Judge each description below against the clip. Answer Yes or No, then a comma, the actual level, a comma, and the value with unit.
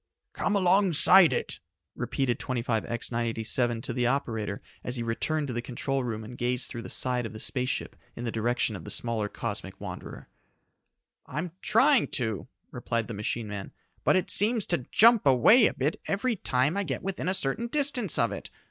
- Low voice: Yes, low, 125 Hz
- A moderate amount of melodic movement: No, wide, 8.0 semitones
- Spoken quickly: No, average, 185 wpm